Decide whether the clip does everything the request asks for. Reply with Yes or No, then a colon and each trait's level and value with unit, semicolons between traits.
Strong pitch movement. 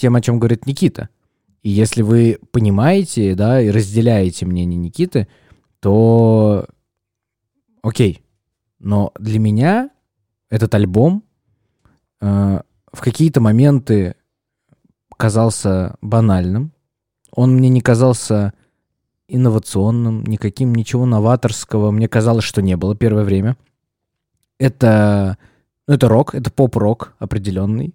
No: average, 3.2 semitones